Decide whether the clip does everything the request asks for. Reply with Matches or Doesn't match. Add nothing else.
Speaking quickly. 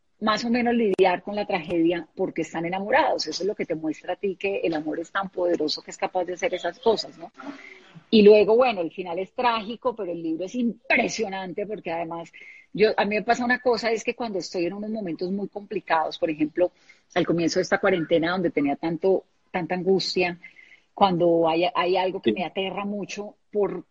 Matches